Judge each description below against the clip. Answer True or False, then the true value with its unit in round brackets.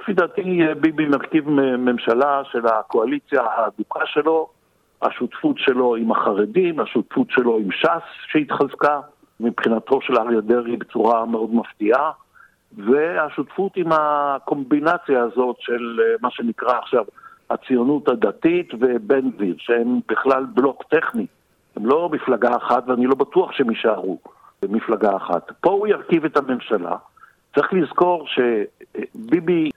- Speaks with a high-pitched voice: False (140 Hz)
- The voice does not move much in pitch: False (5.2 semitones)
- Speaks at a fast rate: False (120 wpm)